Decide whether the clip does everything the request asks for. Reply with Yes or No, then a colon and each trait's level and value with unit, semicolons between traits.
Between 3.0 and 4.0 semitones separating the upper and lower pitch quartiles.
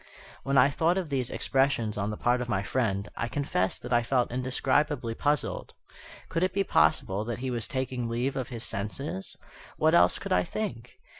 Yes: average, 3.6 semitones